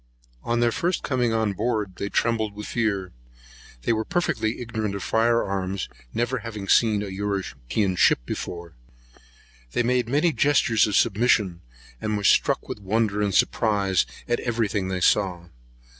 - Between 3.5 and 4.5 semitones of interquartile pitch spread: No, average, 3.1 semitones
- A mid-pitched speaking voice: No, low, 105 Hz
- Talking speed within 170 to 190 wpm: No, average, 160 wpm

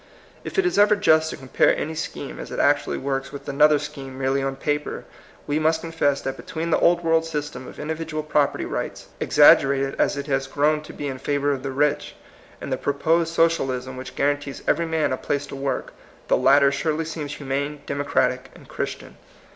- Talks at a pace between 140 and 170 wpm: No, average, 195 wpm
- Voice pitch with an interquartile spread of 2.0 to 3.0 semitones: Yes, narrow, 2.5 semitones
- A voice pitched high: No, medium, 145 Hz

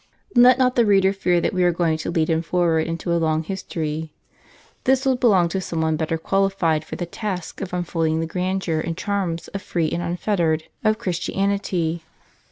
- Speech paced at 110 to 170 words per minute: No, average, 195 wpm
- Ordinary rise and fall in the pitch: Yes, average, 3.2 semitones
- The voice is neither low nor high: Yes, medium, 175 Hz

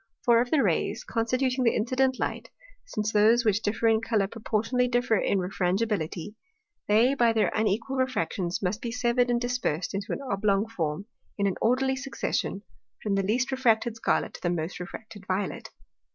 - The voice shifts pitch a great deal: No, average, 3.8 semitones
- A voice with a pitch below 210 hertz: No, high, 225 Hz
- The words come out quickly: No, average, 170 wpm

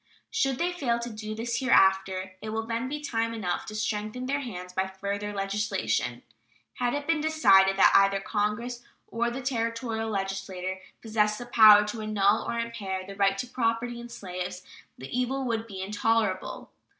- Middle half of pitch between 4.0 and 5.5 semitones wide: No, average, 3.4 semitones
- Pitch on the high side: Yes, high, 215 Hz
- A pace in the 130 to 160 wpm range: No, average, 175 wpm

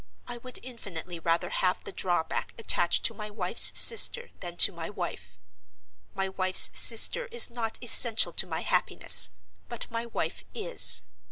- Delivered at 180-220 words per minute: No, average, 155 wpm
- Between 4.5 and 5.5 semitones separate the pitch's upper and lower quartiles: Yes, average, 5.2 semitones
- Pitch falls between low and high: No, high, 210 Hz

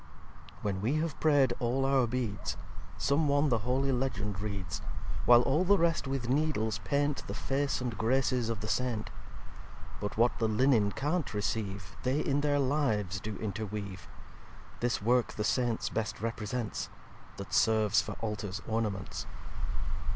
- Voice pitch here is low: Yes, low, 120 Hz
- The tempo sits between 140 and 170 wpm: Yes, average, 150 wpm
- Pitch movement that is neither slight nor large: Yes, average, 4.4 semitones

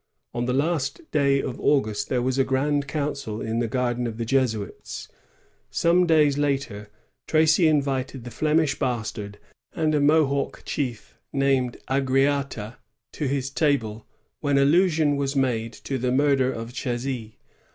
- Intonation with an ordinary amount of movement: Yes, average, 3.1 semitones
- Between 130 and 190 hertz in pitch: Yes, low, 135 Hz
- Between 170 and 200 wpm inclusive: No, average, 145 wpm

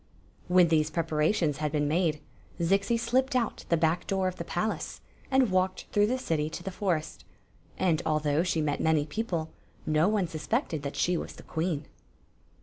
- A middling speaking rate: Yes, average, 175 wpm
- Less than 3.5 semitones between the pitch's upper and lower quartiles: No, average, 3.8 semitones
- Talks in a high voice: No, medium, 170 Hz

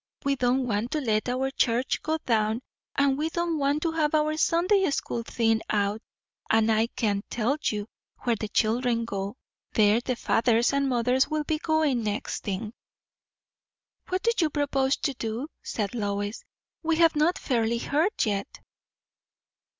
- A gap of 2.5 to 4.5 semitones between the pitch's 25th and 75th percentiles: No, average, 5.3 semitones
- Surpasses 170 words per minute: No, average, 160 wpm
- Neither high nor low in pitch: No, very high, 250 Hz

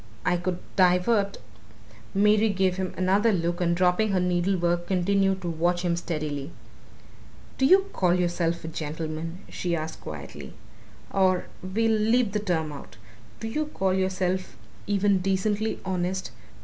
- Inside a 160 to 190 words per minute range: No, average, 145 wpm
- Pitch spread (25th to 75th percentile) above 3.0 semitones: No, narrow, 2.4 semitones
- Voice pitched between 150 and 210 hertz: Yes, medium, 185 Hz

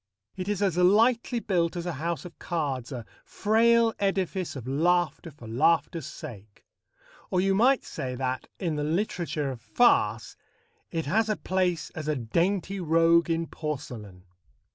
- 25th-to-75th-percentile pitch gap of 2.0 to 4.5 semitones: No, average, 5.0 semitones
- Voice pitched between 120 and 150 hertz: No, medium, 170 Hz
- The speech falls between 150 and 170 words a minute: Yes, average, 155 wpm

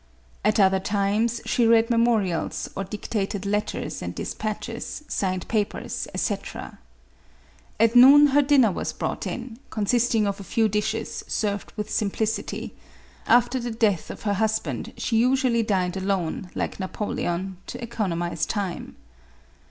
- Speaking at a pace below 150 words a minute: Yes, average, 140 wpm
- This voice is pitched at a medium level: No, high, 215 Hz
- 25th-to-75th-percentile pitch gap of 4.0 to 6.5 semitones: No, average, 3.1 semitones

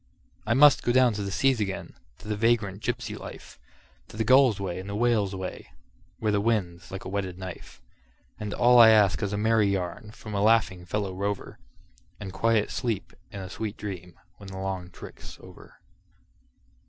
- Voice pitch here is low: Yes, low, 105 Hz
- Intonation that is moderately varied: Yes, average, 3.0 semitones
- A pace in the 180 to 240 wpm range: Yes, average, 190 wpm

